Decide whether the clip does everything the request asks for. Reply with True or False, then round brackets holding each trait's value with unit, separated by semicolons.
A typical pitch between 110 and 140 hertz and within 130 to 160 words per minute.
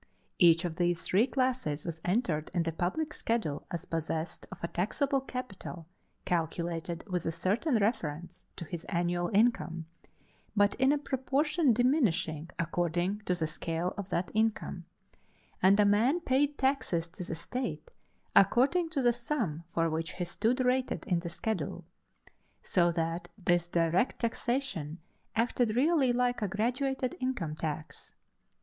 False (190 Hz; 145 wpm)